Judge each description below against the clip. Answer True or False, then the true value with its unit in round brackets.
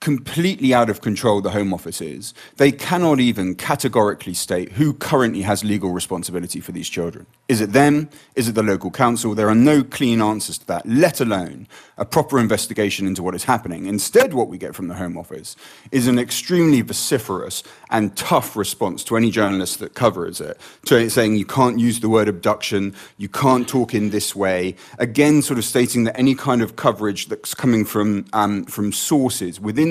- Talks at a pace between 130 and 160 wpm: False (195 wpm)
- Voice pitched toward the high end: False (110 Hz)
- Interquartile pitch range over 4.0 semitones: True (4.5 semitones)